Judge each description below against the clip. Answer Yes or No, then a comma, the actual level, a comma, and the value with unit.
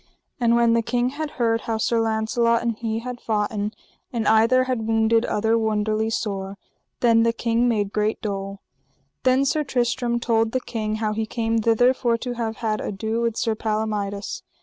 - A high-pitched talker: Yes, high, 225 Hz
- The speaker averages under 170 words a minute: No, average, 180 wpm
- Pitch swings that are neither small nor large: No, narrow, 1.6 semitones